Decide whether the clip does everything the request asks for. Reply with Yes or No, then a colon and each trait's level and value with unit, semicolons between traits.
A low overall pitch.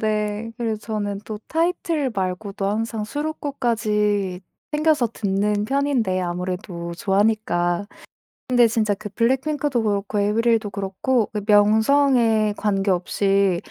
No: high, 210 Hz